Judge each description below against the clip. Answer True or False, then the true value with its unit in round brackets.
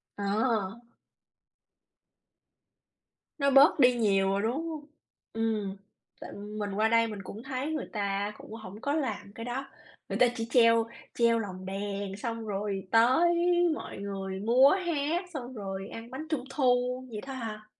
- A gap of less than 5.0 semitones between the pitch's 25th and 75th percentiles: True (4.1 semitones)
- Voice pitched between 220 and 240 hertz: True (225 Hz)